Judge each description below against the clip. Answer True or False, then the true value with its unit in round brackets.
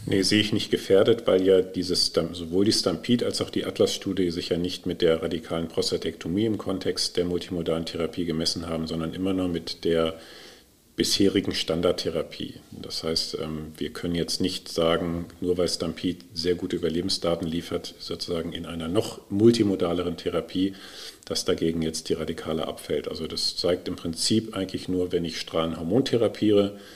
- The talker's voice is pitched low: True (90 Hz)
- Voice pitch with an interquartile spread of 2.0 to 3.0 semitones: True (2.4 semitones)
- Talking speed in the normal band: True (160 wpm)